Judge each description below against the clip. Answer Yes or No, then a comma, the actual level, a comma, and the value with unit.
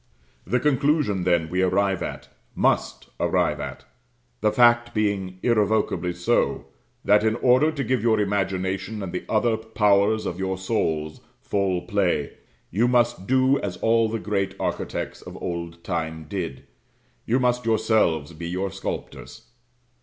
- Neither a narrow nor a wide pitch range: Yes, average, 4.1 semitones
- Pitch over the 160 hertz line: No, low, 100 Hz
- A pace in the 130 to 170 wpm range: Yes, average, 145 wpm